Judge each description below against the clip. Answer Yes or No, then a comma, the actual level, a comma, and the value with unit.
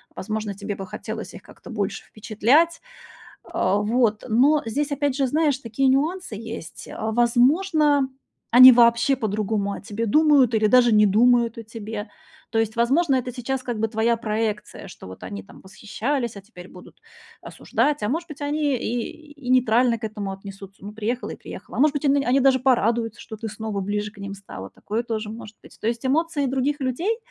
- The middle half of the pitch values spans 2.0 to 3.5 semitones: No, average, 4.2 semitones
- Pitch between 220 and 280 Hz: Yes, high, 235 Hz